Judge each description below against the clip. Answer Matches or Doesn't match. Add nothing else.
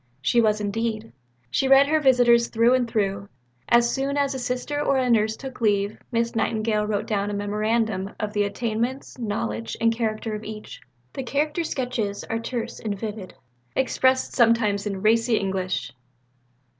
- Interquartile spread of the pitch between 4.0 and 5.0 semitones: Doesn't match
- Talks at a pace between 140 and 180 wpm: Matches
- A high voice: Matches